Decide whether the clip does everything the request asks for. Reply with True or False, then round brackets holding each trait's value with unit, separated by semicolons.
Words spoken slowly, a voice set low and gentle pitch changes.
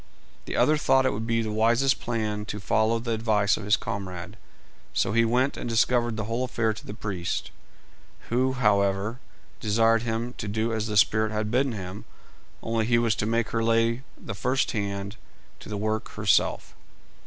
False (185 wpm; 110 Hz; 2.0 semitones)